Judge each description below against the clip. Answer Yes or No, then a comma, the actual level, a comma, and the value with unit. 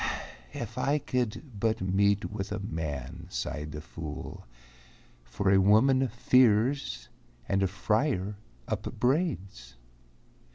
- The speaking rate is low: Yes, slow, 110 wpm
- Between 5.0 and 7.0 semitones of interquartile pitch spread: Yes, average, 5.3 semitones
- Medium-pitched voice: No, low, 100 Hz